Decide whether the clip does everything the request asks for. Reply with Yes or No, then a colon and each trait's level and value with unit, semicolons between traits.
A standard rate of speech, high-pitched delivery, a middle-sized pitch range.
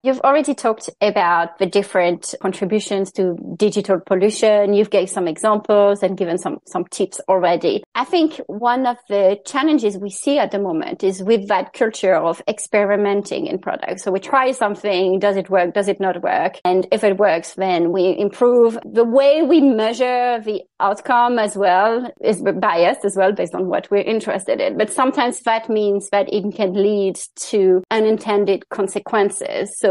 Yes: average, 175 wpm; high, 205 Hz; average, 3.0 semitones